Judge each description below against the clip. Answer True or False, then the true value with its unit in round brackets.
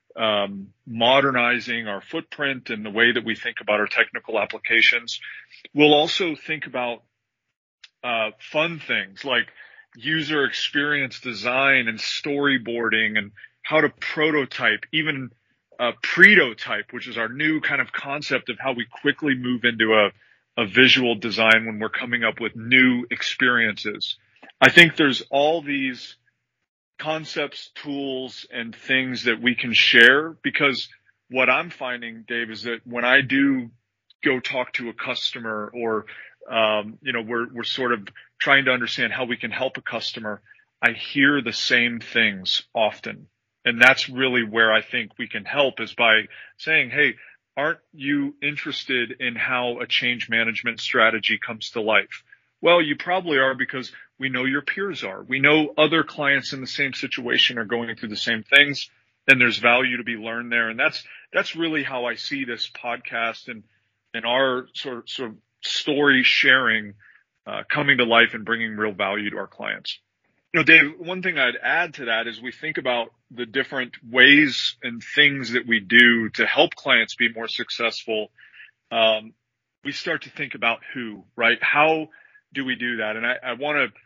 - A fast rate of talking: False (175 wpm)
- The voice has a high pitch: False (125 Hz)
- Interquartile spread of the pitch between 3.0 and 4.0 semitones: True (3.6 semitones)